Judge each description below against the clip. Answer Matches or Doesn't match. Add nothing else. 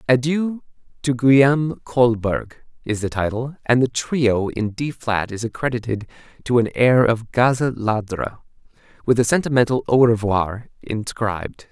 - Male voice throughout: Matches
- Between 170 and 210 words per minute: Doesn't match